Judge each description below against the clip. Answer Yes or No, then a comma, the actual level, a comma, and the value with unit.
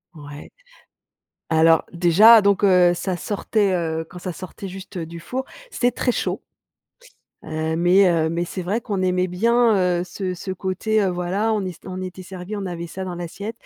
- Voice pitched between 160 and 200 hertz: Yes, medium, 185 Hz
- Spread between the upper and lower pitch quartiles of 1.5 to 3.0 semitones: Yes, average, 2.7 semitones